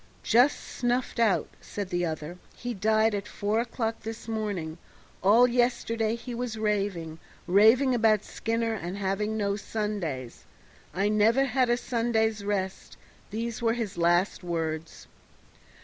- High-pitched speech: Yes, high, 215 Hz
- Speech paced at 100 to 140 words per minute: Yes, slow, 135 wpm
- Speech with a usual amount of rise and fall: Yes, average, 3.3 semitones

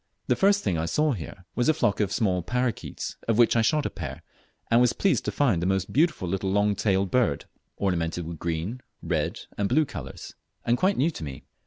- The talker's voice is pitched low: Yes, low, 105 Hz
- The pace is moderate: No, fast, 215 wpm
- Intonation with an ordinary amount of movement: No, wide, 5.9 semitones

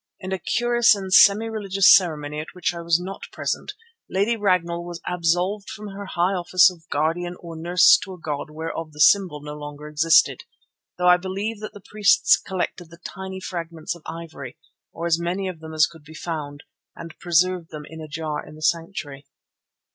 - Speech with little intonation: No, average, 3.1 semitones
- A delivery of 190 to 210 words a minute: Yes, average, 195 wpm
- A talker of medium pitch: Yes, medium, 170 Hz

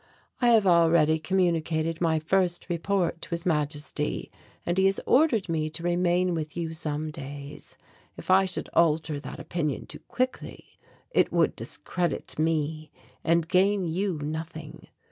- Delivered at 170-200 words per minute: No, average, 150 wpm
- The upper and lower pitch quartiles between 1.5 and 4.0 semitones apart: Yes, average, 2.7 semitones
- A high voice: No, medium, 165 Hz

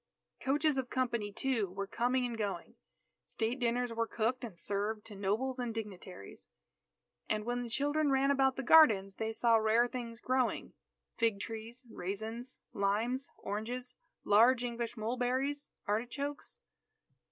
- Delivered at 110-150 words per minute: Yes, average, 140 wpm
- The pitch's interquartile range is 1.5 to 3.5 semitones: Yes, average, 2.9 semitones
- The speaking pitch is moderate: No, high, 235 Hz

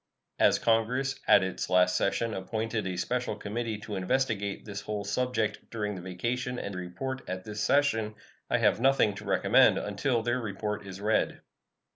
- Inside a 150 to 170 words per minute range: Yes, average, 165 wpm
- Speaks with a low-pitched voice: Yes, low, 105 Hz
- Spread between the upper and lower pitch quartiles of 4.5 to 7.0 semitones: No, average, 3.3 semitones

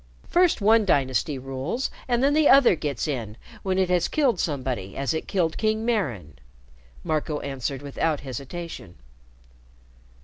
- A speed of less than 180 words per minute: Yes, average, 140 wpm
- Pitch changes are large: Yes, wide, 8.3 semitones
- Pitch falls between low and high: Yes, medium, 155 Hz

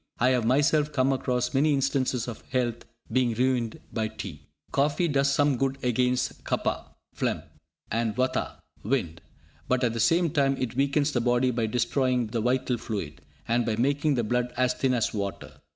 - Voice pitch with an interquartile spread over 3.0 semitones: No, average, 2.7 semitones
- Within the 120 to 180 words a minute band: Yes, average, 175 wpm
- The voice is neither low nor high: No, low, 125 Hz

